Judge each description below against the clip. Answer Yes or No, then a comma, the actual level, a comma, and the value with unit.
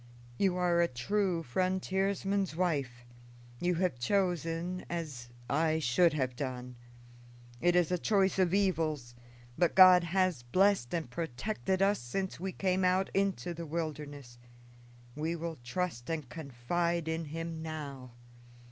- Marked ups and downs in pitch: No, average, 4.3 semitones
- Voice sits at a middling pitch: Yes, medium, 170 Hz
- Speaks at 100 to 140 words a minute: Yes, slow, 135 wpm